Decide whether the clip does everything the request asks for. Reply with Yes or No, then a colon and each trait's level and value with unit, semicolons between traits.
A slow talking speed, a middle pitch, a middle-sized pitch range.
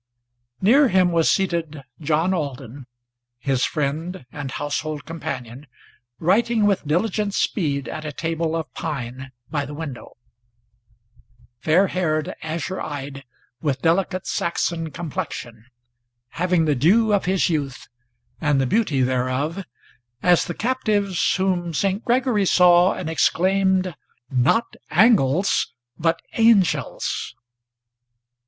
Yes: slow, 115 wpm; medium, 165 Hz; average, 4.8 semitones